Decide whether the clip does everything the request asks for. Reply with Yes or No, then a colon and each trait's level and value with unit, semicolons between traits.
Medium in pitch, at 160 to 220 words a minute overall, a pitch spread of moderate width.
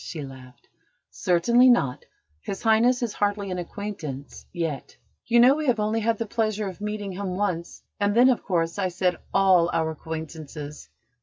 No: high, 195 Hz; average, 170 wpm; average, 4.8 semitones